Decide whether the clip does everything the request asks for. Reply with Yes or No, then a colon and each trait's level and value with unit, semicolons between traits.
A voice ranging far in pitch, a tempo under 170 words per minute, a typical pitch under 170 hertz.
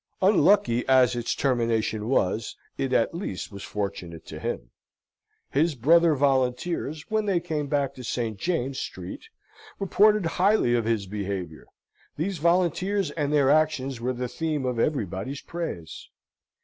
Yes: wide, 6.4 semitones; average, 140 wpm; low, 135 Hz